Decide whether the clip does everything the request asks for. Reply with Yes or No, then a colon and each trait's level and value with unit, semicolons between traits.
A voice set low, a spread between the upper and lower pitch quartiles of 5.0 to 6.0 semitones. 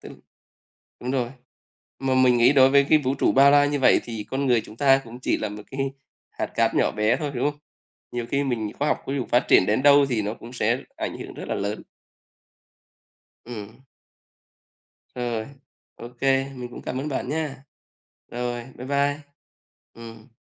No: low, 130 Hz; average, 2.8 semitones